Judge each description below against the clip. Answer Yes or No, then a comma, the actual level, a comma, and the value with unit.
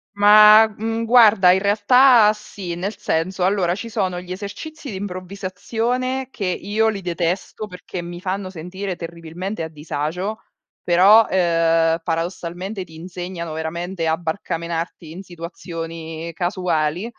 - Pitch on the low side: No, medium, 185 Hz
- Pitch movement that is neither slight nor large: Yes, average, 3.5 semitones